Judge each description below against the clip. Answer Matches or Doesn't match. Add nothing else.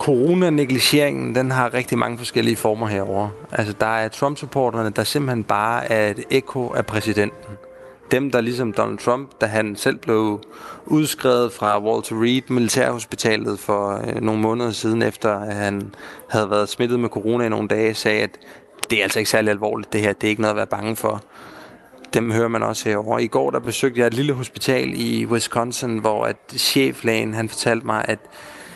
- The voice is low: Matches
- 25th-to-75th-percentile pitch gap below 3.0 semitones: Matches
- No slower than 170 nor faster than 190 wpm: Matches